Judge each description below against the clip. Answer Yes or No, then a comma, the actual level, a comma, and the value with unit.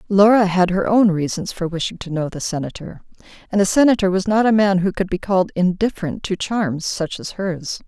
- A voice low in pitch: No, high, 190 Hz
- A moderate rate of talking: No, fast, 215 wpm